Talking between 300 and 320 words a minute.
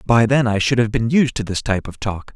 Yes: fast, 305 wpm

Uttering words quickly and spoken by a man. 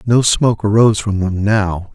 No: average, 185 wpm; male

